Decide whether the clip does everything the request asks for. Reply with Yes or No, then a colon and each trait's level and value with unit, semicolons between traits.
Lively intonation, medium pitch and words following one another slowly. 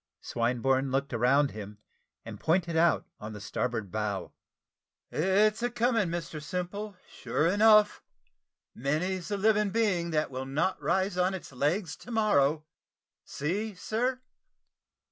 Yes: wide, 7.1 semitones; medium, 170 Hz; slow, 130 wpm